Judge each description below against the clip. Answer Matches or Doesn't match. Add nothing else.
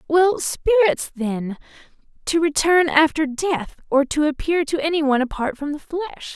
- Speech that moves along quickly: Doesn't match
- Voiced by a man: Doesn't match